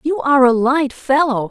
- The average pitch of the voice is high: Yes, very high, 270 Hz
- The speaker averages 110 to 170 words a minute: No, average, 200 wpm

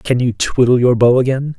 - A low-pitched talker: Yes, low, 125 Hz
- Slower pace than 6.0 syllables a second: Yes, 5.2 syllables/s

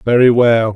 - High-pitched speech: No, low, 115 Hz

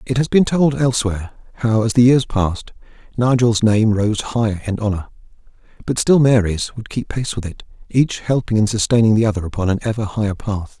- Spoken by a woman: No, male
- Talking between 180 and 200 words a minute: Yes, average, 195 wpm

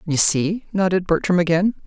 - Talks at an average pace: Yes, average, 160 wpm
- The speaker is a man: No, female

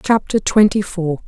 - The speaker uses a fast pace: No, average, 140 wpm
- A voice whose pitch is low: No, high, 195 Hz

